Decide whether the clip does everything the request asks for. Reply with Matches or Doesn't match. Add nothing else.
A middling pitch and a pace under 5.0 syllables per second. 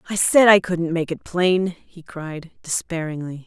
Matches